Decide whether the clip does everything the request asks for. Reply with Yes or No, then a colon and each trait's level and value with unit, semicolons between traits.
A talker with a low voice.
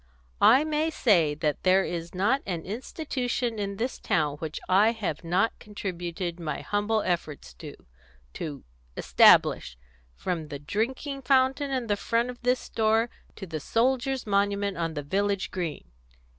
No: high, 200 Hz